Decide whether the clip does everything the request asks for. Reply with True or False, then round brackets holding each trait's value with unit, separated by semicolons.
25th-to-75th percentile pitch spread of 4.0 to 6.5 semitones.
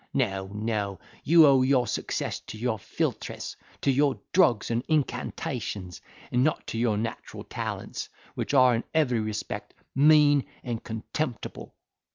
True (4.6 semitones)